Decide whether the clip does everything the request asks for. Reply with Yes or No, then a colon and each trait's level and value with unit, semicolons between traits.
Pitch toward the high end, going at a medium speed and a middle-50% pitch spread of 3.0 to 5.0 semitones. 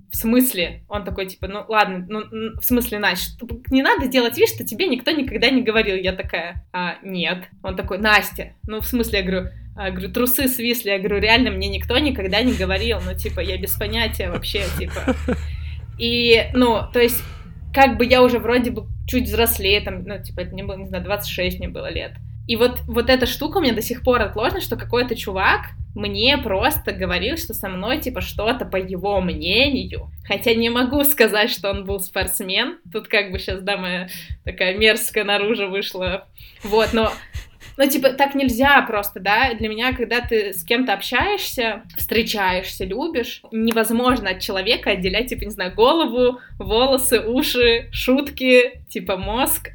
No: high, 225 Hz; fast, 180 wpm; average, 3.9 semitones